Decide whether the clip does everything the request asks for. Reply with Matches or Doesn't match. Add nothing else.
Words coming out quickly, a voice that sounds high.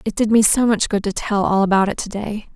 Matches